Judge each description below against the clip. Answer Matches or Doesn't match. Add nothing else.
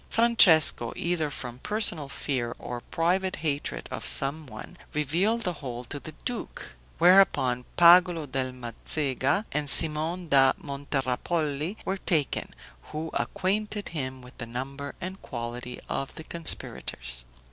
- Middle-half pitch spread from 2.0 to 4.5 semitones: Doesn't match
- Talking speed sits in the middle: Doesn't match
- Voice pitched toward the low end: Doesn't match